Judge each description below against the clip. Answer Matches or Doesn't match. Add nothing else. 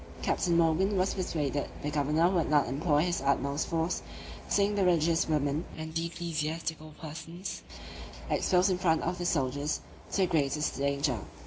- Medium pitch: Matches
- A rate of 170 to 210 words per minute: Doesn't match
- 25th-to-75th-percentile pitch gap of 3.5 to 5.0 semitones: Doesn't match